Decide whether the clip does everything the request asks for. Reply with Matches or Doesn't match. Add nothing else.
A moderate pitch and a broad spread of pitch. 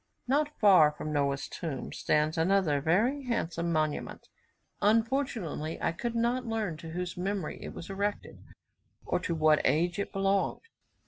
Matches